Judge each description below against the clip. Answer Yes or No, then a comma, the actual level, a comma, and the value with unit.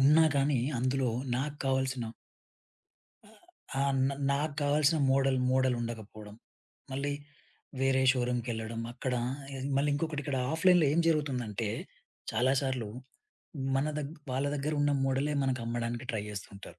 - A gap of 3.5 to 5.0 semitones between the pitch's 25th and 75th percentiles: No, average, 3.1 semitones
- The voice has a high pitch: No, low, 130 Hz